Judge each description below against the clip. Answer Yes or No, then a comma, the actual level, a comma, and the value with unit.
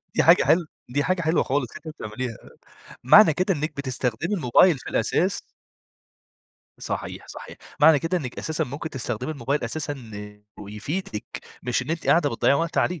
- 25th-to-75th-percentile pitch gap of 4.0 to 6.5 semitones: Yes, average, 4.9 semitones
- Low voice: No, medium, 145 Hz